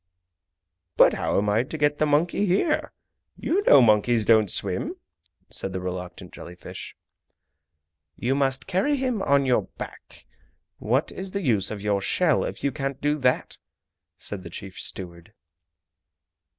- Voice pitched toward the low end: Yes, low, 130 Hz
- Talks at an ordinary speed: Yes, average, 150 wpm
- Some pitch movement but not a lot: No, wide, 7.3 semitones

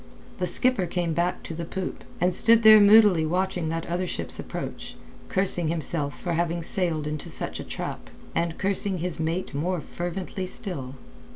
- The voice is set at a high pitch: No, medium, 175 Hz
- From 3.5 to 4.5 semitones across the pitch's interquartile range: No, narrow, 2.4 semitones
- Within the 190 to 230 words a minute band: No, average, 170 wpm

